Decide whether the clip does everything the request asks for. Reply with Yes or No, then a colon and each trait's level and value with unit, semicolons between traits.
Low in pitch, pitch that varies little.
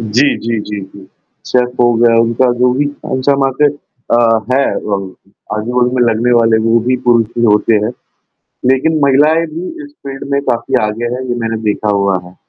No: low, 120 Hz; average, 3.2 semitones